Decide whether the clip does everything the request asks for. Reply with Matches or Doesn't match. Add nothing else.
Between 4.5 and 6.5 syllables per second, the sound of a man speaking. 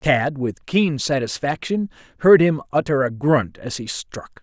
Doesn't match